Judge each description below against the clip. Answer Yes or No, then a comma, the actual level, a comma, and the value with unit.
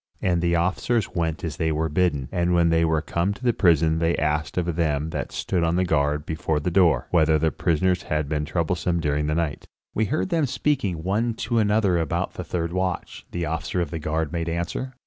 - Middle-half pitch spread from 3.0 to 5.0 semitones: No, narrow, 2.6 semitones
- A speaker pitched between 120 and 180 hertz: No, very low, 85 Hz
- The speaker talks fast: Yes, fast, 215 wpm